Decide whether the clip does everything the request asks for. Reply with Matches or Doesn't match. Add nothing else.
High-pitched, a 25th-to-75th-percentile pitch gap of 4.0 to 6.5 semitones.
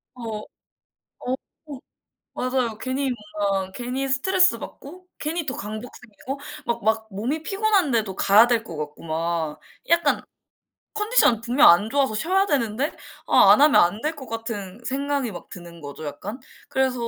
Matches